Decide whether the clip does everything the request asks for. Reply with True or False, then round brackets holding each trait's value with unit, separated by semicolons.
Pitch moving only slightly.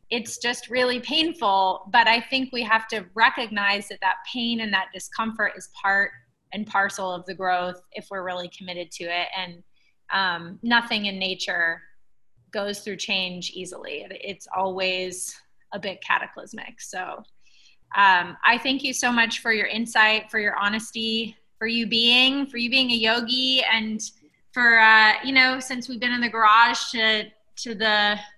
False (3.8 semitones)